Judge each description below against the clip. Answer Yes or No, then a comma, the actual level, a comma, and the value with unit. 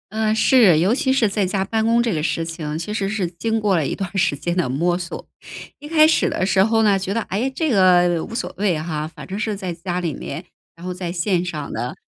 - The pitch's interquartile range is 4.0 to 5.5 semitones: Yes, average, 4.3 semitones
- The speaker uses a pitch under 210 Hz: Yes, high, 190 Hz